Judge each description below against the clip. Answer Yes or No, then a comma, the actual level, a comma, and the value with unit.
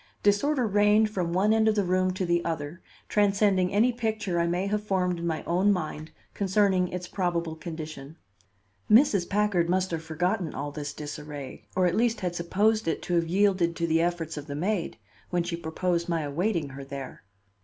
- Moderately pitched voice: Yes, medium, 180 Hz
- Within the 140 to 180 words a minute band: No, average, 190 wpm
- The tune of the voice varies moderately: Yes, average, 3.8 semitones